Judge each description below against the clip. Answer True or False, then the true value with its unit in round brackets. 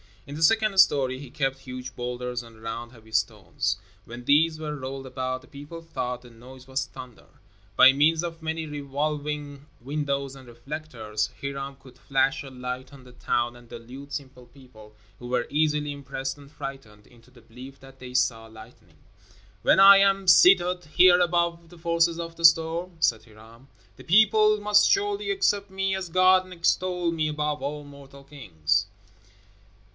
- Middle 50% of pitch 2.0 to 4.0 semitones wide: False (4.7 semitones)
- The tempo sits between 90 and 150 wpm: False (170 wpm)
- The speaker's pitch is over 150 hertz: False (140 Hz)